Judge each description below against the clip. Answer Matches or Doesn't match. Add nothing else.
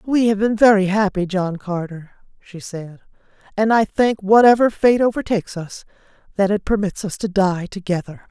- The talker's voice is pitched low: Doesn't match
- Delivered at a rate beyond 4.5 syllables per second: Matches